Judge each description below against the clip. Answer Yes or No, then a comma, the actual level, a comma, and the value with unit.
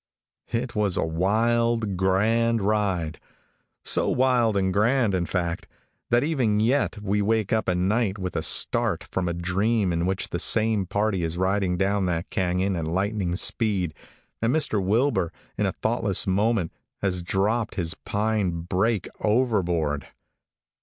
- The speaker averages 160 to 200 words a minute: No, average, 150 wpm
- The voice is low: Yes, low, 100 Hz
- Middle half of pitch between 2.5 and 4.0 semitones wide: Yes, average, 3.7 semitones